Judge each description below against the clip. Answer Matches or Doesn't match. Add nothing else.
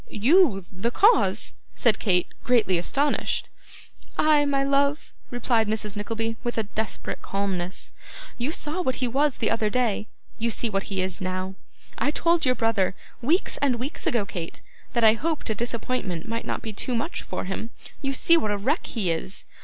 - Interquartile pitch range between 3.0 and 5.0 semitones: Doesn't match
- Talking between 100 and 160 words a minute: Doesn't match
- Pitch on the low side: Doesn't match